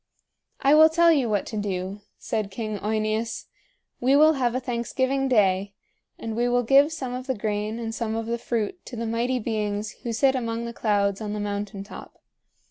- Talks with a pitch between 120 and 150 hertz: No, high, 230 Hz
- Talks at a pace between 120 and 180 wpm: No, average, 200 wpm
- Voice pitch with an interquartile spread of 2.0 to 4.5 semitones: Yes, average, 3.4 semitones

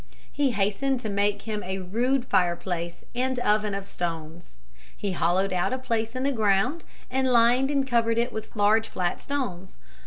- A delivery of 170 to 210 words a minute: Yes, average, 175 wpm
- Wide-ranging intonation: No, average, 5.0 semitones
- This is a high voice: Yes, high, 215 Hz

